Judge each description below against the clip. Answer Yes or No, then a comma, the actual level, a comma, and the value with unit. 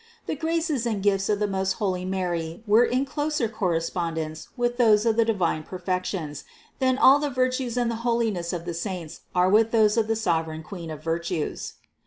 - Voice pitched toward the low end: No, high, 205 Hz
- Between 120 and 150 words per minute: No, average, 190 wpm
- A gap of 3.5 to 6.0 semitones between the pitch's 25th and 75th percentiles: Yes, wide, 5.4 semitones